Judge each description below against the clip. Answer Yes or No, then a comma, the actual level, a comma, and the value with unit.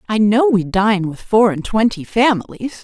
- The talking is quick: No, average, 190 wpm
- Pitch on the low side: No, high, 210 Hz